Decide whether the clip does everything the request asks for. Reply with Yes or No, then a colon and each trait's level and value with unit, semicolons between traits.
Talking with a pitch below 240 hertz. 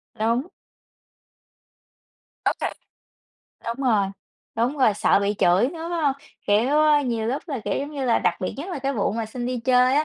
No: very high, 250 Hz